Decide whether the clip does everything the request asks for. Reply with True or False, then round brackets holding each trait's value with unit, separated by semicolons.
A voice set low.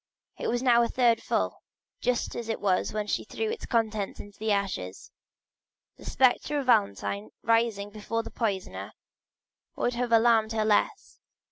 False (225 Hz)